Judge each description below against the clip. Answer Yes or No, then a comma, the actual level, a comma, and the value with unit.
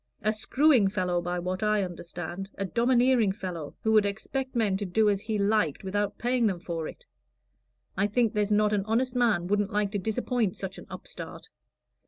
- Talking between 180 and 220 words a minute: Yes, average, 190 wpm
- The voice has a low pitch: No, high, 205 Hz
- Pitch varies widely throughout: No, average, 3.0 semitones